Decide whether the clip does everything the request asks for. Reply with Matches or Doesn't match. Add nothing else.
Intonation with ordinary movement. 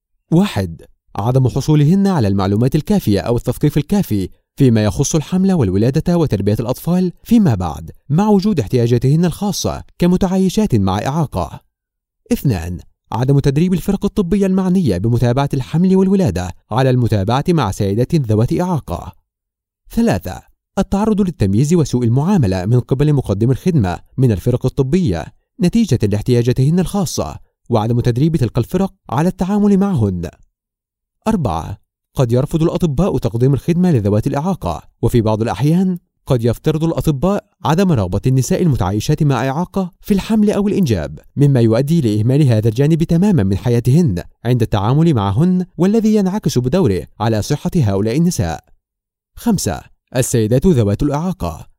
Doesn't match